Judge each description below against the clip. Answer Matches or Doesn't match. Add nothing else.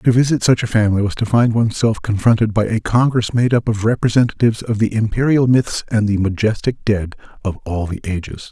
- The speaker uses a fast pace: Matches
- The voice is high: Doesn't match